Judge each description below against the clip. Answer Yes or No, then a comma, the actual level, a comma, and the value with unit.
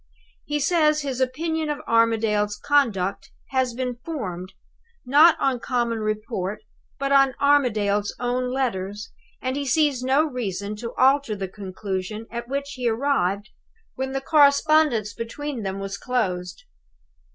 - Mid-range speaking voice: No, high, 245 Hz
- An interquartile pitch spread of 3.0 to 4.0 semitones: No, average, 5.1 semitones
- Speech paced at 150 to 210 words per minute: No, slow, 135 wpm